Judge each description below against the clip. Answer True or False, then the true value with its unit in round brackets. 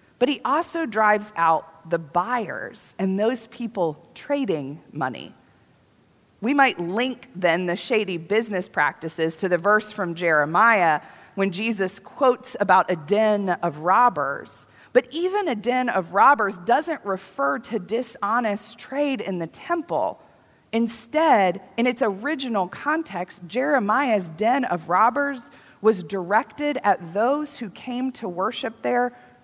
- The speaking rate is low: True (130 wpm)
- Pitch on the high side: True (215 Hz)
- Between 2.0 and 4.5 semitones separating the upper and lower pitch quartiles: False (5.6 semitones)